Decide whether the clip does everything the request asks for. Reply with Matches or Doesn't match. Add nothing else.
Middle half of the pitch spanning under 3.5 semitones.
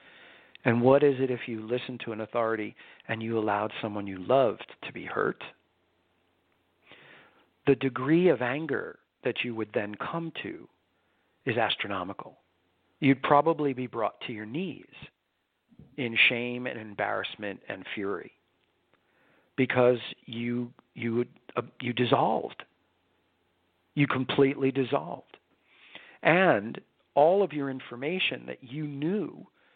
Doesn't match